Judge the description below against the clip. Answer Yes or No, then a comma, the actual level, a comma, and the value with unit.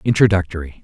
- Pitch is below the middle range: Yes, very low, 90 Hz